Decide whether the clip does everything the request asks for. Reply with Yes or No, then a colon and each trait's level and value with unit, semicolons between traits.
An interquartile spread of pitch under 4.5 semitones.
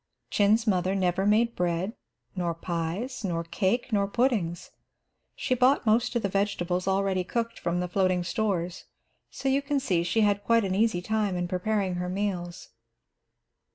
Yes: average, 3.8 semitones